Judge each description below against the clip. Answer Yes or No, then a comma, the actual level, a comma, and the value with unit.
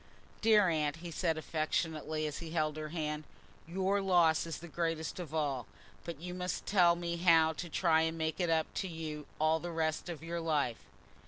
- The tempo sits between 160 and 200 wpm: Yes, average, 195 wpm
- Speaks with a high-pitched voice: No, medium, 165 Hz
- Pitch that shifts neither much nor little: No, narrow, 1.8 semitones